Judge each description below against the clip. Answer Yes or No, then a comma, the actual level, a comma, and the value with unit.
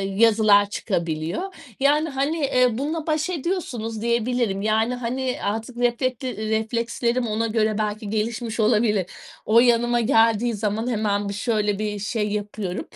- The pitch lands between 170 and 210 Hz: No, high, 225 Hz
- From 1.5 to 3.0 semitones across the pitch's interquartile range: Yes, average, 2.7 semitones